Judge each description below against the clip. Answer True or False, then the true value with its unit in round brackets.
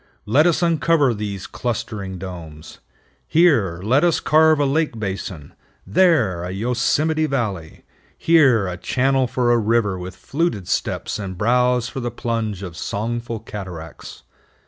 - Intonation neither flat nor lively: False (6.2 semitones)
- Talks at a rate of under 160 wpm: True (140 wpm)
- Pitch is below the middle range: True (115 Hz)